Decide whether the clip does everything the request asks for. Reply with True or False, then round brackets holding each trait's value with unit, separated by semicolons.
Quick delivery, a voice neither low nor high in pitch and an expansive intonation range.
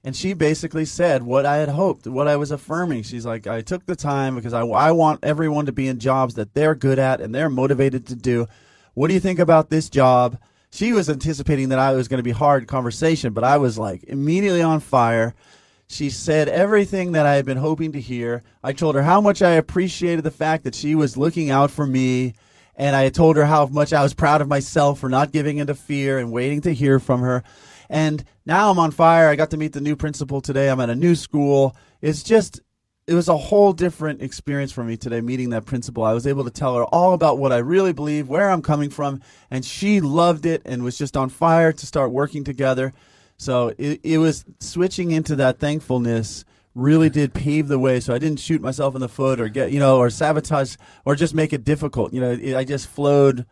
False (235 wpm; 145 Hz; 3.4 semitones)